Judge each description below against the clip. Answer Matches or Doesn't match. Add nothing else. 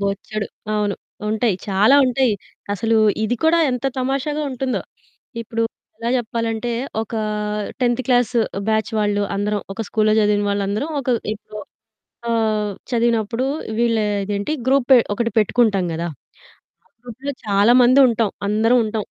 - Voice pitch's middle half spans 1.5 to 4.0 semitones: Matches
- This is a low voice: Doesn't match